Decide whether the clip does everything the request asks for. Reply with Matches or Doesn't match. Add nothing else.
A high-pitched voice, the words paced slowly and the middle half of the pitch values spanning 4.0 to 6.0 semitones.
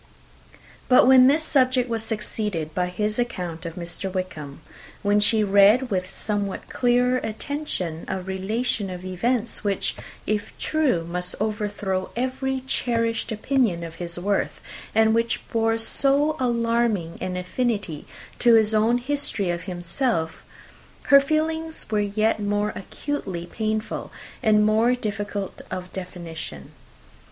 Matches